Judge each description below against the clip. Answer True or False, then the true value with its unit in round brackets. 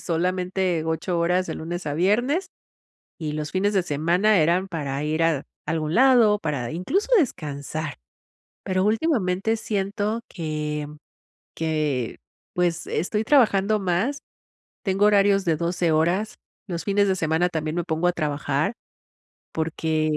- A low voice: False (175 Hz)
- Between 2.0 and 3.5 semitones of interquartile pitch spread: False (4.2 semitones)